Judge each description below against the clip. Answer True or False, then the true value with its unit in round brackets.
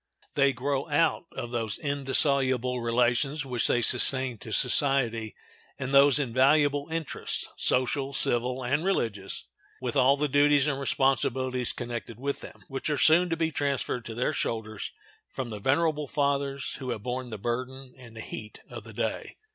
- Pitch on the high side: False (130 Hz)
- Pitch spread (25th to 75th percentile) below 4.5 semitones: True (2.8 semitones)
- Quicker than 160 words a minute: False (155 wpm)